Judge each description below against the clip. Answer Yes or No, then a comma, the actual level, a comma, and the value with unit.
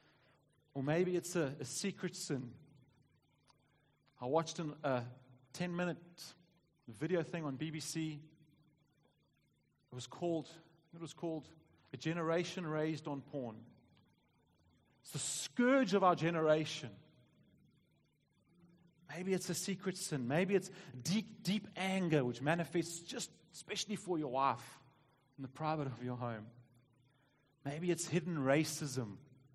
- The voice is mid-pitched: Yes, medium, 155 Hz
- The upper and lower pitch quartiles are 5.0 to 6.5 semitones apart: No, average, 4.1 semitones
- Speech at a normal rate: No, slow, 125 wpm